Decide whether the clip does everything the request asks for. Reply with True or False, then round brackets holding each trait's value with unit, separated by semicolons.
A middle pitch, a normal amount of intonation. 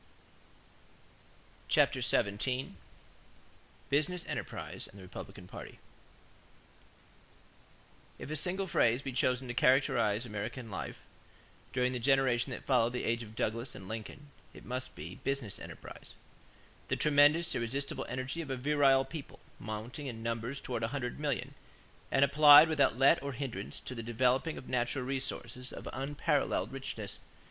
False (130 Hz; 3.3 semitones)